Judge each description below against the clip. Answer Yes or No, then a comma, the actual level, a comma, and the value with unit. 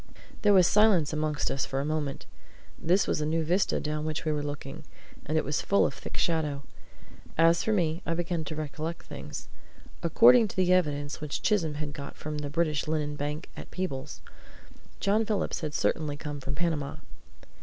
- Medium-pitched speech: Yes, medium, 155 Hz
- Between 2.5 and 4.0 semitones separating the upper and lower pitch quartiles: Yes, average, 2.9 semitones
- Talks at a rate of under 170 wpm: No, average, 185 wpm